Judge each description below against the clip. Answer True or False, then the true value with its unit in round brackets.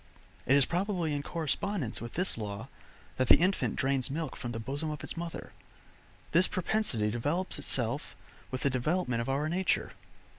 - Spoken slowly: False (170 wpm)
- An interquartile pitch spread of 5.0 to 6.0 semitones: True (5.6 semitones)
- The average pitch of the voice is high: False (145 Hz)